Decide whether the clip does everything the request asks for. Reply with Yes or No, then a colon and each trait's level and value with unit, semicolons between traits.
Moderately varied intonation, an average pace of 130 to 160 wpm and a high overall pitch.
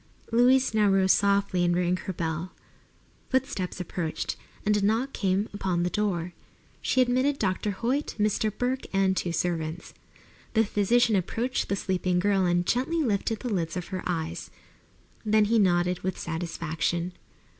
Yes: average, 3.8 semitones; average, 155 wpm; high, 195 Hz